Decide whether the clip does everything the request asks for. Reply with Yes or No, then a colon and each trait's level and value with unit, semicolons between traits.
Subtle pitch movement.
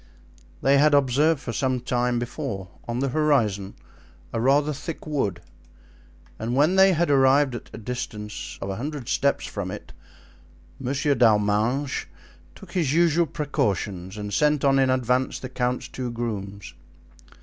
No: average, 4.6 semitones